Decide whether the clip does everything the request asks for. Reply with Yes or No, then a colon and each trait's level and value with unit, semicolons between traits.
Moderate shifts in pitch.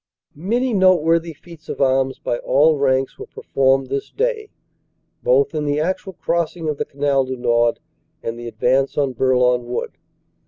Yes: average, 4.5 semitones